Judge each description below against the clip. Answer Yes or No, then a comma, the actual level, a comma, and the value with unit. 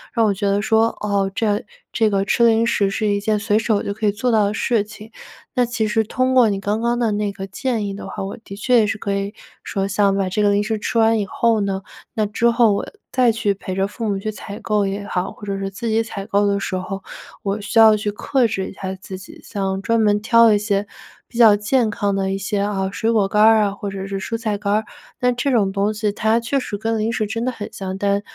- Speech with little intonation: Yes, narrow, 2.1 semitones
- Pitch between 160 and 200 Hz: No, high, 210 Hz